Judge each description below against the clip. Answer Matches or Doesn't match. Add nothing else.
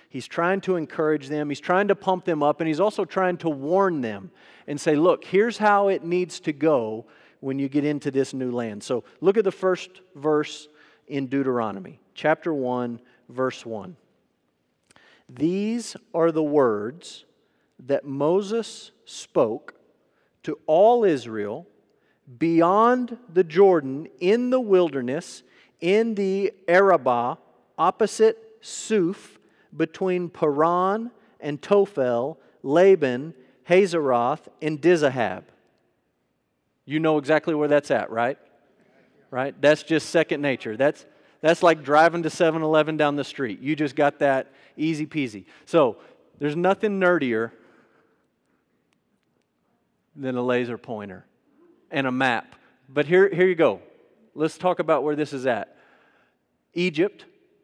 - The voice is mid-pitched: Matches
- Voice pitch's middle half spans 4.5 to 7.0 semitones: Matches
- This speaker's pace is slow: Matches